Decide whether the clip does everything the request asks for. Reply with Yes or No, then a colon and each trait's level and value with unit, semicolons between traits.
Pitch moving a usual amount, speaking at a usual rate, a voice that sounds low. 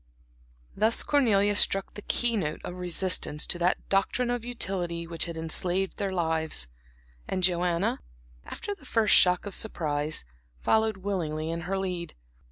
No: average, 3.5 semitones; average, 150 wpm; medium, 185 Hz